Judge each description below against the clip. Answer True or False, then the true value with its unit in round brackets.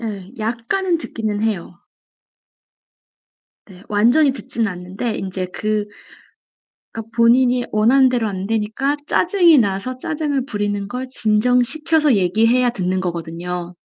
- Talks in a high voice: True (225 Hz)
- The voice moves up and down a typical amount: True (4.4 semitones)